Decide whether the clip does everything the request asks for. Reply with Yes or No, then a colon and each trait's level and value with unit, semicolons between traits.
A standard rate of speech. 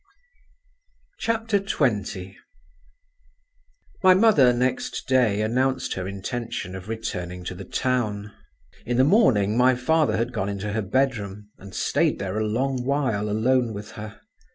No: slow, 130 wpm